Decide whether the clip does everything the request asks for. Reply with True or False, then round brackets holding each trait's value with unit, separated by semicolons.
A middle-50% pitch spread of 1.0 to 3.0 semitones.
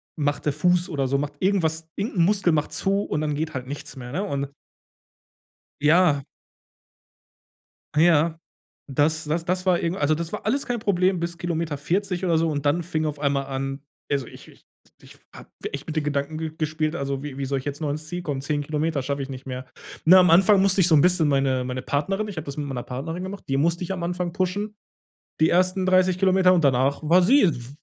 False (4.2 semitones)